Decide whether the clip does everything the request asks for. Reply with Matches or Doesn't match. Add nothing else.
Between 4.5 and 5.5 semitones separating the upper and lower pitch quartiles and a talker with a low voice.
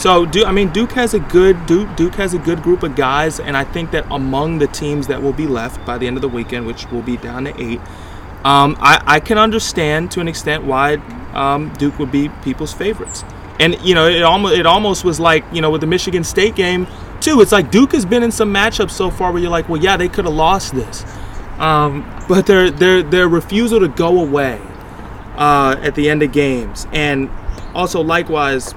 Doesn't match